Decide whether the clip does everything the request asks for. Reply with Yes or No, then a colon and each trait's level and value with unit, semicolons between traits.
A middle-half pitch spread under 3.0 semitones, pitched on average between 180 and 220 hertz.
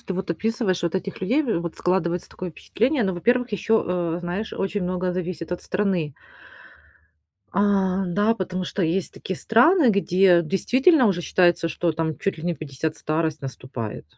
No: average, 3.3 semitones; medium, 185 Hz